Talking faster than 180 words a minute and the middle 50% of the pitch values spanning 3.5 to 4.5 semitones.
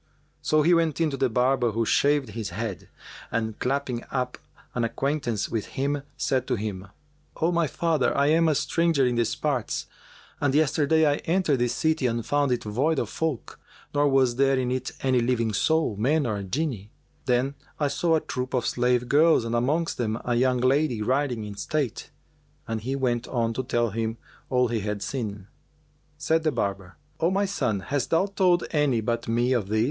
Yes: average, 195 wpm; average, 4.2 semitones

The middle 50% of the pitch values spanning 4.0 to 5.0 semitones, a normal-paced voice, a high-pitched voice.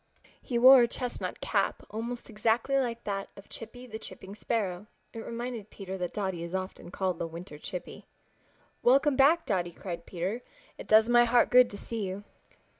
Yes: average, 4.3 semitones; average, 180 wpm; high, 220 Hz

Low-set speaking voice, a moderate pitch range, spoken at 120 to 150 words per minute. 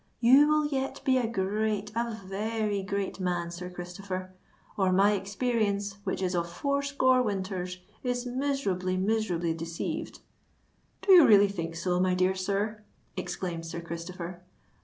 No: high, 195 Hz; average, 3.9 semitones; average, 140 wpm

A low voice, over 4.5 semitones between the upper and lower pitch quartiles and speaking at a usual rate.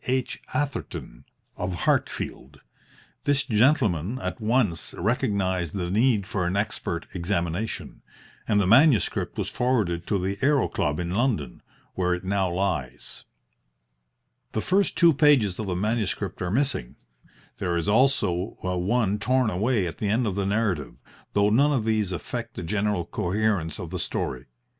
Yes: low, 100 Hz; average, 5.1 semitones; average, 150 wpm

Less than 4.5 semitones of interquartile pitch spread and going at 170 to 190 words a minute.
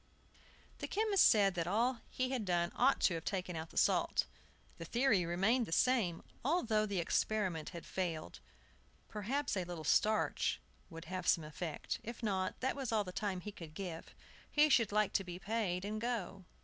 No: average, 4.8 semitones; average, 185 wpm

